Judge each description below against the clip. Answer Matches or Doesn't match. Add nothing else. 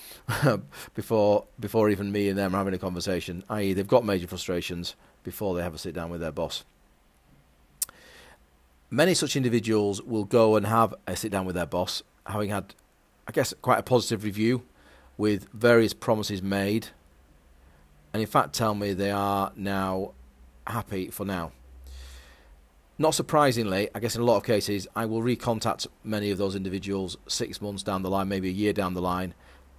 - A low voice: Matches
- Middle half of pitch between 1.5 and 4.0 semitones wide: Matches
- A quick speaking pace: Doesn't match